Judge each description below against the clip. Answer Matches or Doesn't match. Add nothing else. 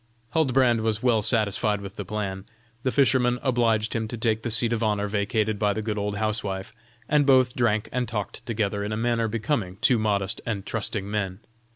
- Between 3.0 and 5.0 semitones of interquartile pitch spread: Doesn't match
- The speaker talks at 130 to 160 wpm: Doesn't match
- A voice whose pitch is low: Matches